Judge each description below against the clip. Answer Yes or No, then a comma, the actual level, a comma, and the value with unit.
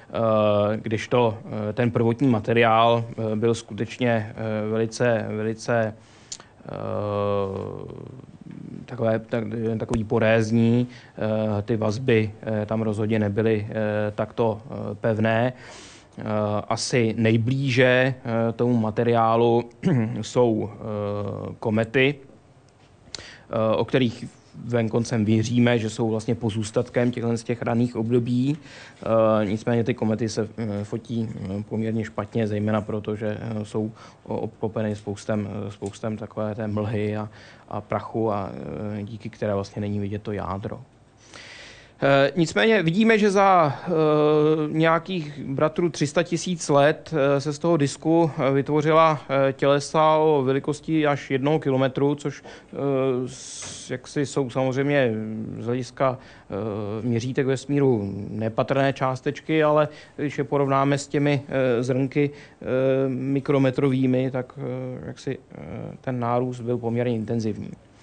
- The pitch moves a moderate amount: Yes, average, 3.8 semitones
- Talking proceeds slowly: Yes, slow, 105 wpm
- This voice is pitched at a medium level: No, low, 120 Hz